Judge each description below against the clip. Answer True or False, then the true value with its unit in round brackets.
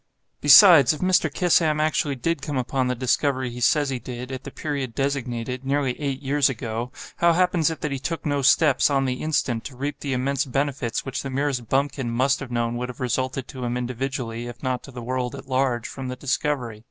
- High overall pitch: False (135 Hz)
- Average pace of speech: False (210 wpm)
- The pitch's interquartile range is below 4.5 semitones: True (2.5 semitones)